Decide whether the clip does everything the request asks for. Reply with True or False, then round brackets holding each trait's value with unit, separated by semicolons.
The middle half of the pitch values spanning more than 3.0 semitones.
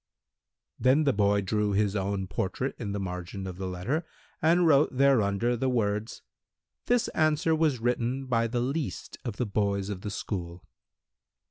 True (5.2 semitones)